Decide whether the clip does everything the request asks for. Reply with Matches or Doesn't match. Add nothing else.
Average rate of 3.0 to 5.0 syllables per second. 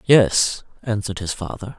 Matches